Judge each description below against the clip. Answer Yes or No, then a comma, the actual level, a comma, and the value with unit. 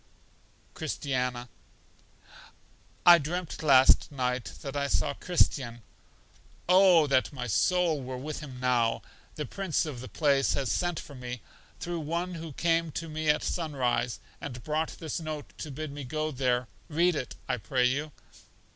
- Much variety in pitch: No, average, 4.1 semitones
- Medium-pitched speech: Yes, medium, 145 Hz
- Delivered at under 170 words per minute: Yes, average, 155 wpm